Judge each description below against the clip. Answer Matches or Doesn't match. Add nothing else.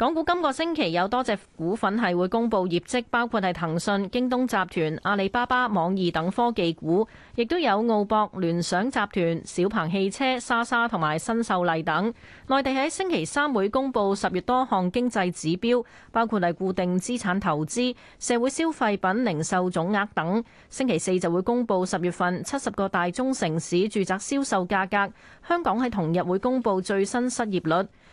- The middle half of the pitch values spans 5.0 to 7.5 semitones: Matches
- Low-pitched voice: Doesn't match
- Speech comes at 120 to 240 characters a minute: Doesn't match